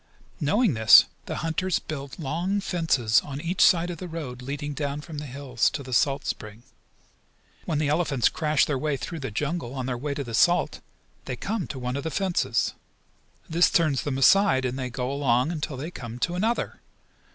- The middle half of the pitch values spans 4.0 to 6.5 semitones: Yes, average, 4.3 semitones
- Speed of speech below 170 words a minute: No, average, 195 wpm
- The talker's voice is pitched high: No, medium, 145 Hz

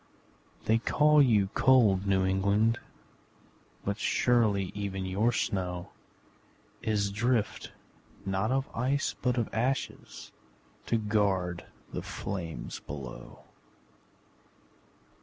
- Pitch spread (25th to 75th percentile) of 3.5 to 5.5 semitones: Yes, average, 3.8 semitones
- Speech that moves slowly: Yes, slow, 95 wpm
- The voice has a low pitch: Yes, low, 105 Hz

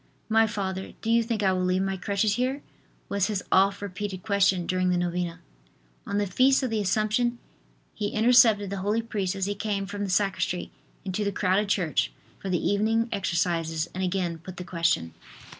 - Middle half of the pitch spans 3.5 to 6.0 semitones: No, narrow, 2.6 semitones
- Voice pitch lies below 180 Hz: No, high, 195 Hz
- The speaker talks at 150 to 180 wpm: No, average, 190 wpm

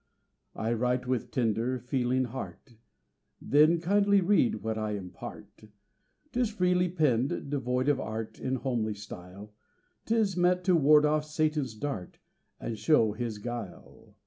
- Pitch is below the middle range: Yes, low, 130 Hz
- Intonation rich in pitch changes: Yes, wide, 5.9 semitones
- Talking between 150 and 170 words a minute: No, slow, 135 wpm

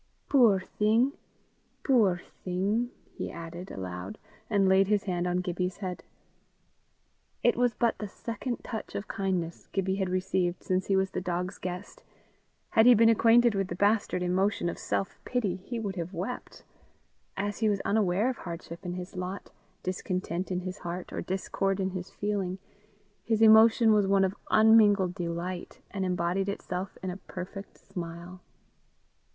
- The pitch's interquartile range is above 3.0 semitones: No, average, 2.7 semitones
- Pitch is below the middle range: No, high, 190 Hz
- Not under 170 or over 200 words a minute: No, average, 160 wpm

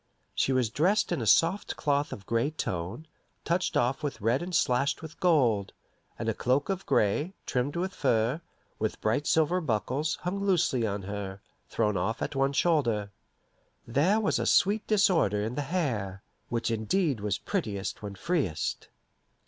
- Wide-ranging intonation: Yes, wide, 7.6 semitones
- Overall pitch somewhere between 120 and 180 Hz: Yes, low, 135 Hz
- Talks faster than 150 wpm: Yes, average, 165 wpm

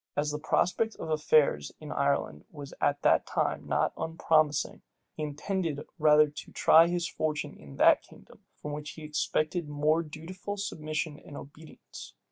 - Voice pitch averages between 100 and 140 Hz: No, medium, 155 Hz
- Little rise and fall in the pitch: Yes, narrow, 1.6 semitones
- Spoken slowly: No, average, 155 wpm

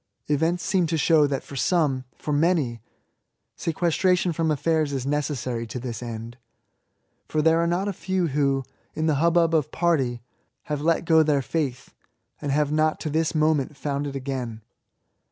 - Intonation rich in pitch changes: No, average, 3.3 semitones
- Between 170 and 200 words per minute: Yes, average, 180 wpm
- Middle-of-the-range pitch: Yes, medium, 150 Hz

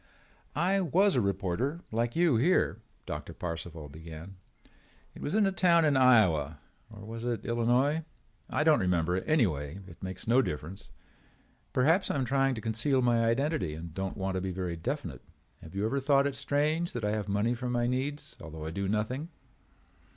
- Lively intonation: Yes, wide, 7.1 semitones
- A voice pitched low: Yes, low, 115 Hz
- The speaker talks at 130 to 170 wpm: No, average, 185 wpm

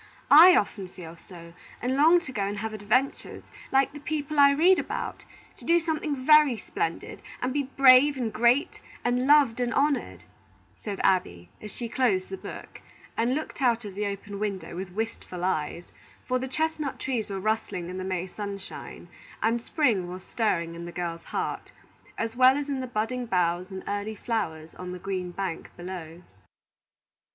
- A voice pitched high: Yes, high, 220 Hz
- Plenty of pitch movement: Yes, wide, 6.2 semitones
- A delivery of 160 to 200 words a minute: Yes, average, 180 wpm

